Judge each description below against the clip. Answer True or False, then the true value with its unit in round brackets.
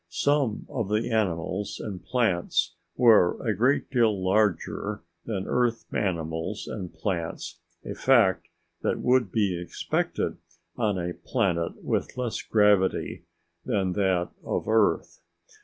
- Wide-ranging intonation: False (4.0 semitones)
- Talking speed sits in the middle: False (125 wpm)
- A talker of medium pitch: False (105 Hz)